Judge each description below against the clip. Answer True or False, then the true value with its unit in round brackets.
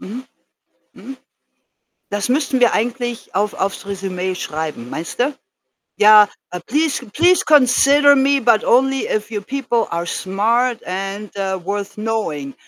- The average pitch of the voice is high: True (220 Hz)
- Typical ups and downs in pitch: True (5.0 semitones)